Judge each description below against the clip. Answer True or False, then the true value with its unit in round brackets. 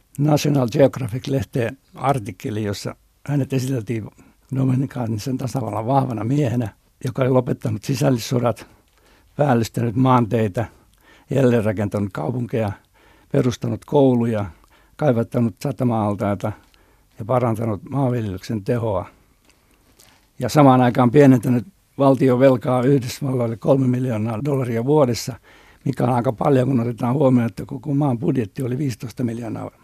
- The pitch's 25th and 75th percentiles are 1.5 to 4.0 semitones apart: True (2.8 semitones)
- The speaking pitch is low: True (125 Hz)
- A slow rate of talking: False (105 wpm)